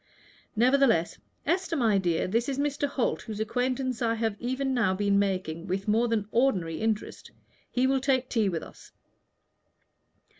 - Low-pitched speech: No, high, 230 Hz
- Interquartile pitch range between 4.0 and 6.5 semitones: Yes, average, 4.6 semitones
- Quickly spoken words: No, average, 150 wpm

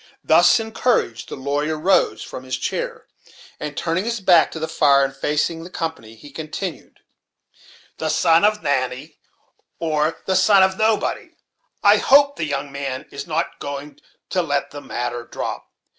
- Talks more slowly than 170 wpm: Yes, average, 160 wpm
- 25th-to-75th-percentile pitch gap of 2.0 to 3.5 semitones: No, average, 4.6 semitones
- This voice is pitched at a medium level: Yes, medium, 155 Hz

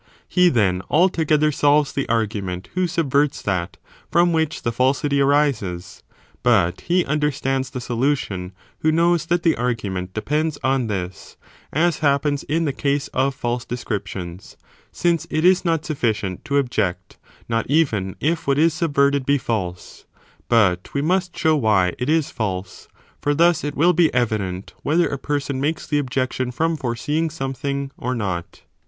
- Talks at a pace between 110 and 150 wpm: No, average, 160 wpm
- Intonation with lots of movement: Yes, wide, 5.9 semitones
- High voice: No, medium, 140 Hz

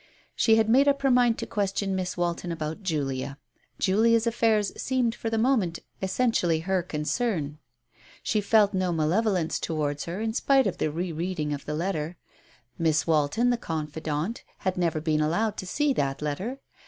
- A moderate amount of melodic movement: No, wide, 6.2 semitones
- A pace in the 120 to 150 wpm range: No, average, 175 wpm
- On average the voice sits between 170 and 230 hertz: Yes, medium, 185 Hz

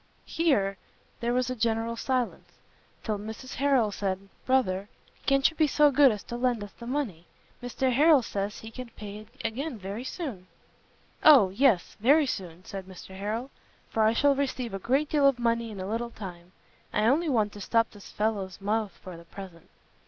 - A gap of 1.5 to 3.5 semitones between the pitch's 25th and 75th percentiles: No, average, 4.8 semitones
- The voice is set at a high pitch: Yes, high, 225 Hz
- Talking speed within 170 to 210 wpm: Yes, average, 190 wpm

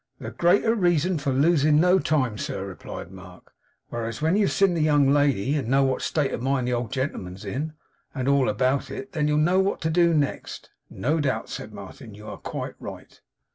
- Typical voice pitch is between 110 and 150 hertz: Yes, medium, 140 Hz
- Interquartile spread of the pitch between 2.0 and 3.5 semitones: No, average, 4.1 semitones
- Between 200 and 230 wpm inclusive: Yes, fast, 205 wpm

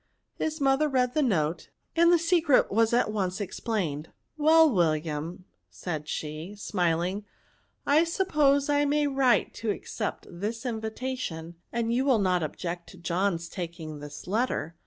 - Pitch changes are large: Yes, wide, 8.1 semitones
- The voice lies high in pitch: Yes, high, 215 Hz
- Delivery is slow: No, average, 155 wpm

